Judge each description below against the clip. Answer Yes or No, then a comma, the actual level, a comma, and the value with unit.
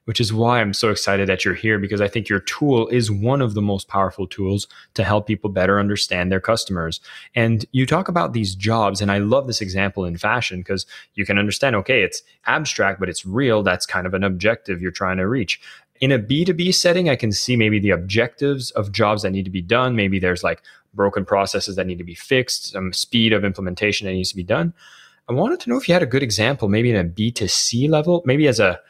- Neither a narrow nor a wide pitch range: Yes, average, 4.0 semitones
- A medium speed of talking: No, fast, 235 wpm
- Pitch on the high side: No, low, 105 Hz